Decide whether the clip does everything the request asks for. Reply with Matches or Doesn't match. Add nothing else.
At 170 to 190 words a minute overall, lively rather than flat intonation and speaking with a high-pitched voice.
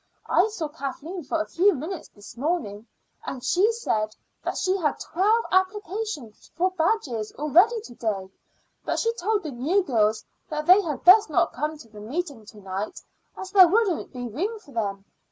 Matches